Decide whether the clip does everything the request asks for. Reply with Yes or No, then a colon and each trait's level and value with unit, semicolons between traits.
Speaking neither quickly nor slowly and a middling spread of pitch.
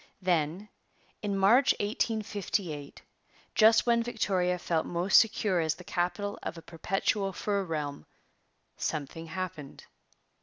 No: slow, 115 wpm; average, 4.1 semitones